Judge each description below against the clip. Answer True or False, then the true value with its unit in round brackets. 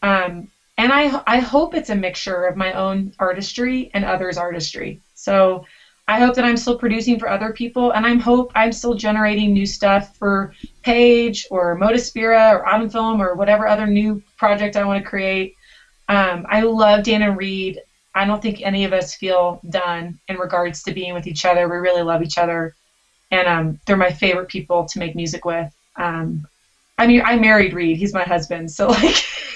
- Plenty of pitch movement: False (3.6 semitones)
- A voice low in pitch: False (195 Hz)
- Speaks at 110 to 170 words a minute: False (195 wpm)